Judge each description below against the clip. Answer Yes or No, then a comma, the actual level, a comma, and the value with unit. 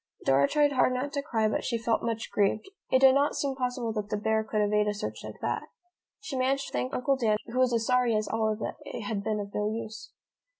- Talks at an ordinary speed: No, fast, 250 wpm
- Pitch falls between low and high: No, high, 225 Hz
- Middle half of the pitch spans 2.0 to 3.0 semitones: No, average, 3.4 semitones